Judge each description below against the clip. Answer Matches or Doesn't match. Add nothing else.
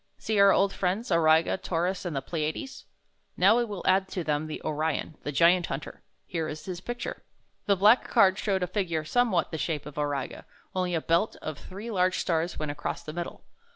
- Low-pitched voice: Doesn't match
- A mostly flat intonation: Doesn't match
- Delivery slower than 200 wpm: Doesn't match